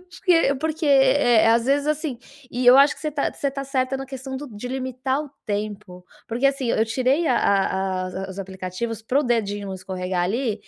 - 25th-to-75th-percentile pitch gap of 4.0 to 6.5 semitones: Yes, average, 5.1 semitones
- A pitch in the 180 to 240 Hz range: No, very high, 250 Hz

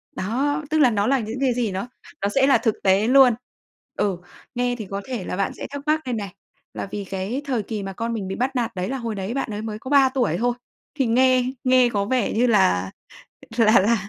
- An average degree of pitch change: Yes, average, 4.2 semitones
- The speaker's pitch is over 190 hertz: Yes, high, 230 Hz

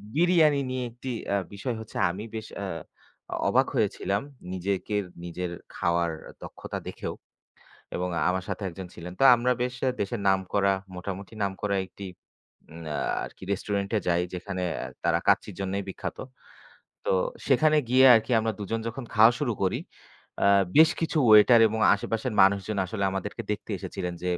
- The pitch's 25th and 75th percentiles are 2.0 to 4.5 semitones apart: Yes, average, 3.7 semitones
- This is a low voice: Yes, low, 100 Hz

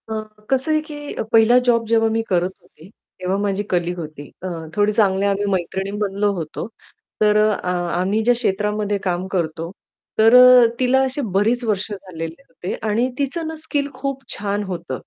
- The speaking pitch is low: No, high, 210 Hz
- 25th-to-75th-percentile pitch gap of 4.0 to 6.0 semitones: Yes, average, 4.6 semitones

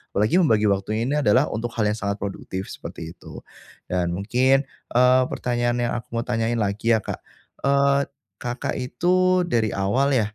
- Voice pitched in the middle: No, low, 120 Hz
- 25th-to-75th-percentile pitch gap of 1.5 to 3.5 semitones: No, average, 4.0 semitones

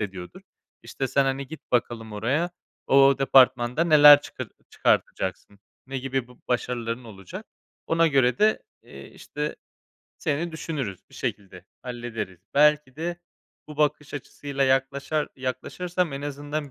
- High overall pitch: No, low, 135 Hz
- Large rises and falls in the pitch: No, average, 3.7 semitones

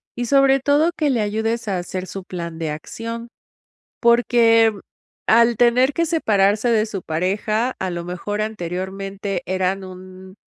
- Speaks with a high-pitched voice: Yes, high, 210 Hz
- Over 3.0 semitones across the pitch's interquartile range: Yes, average, 4.0 semitones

